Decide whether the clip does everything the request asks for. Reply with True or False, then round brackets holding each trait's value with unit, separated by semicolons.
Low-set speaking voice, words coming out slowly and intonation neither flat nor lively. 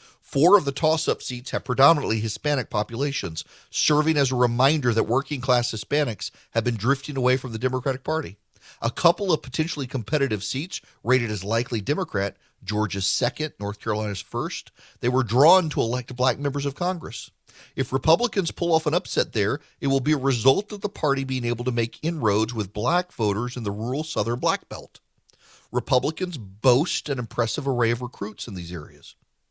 False (130 Hz; 175 wpm; 4.5 semitones)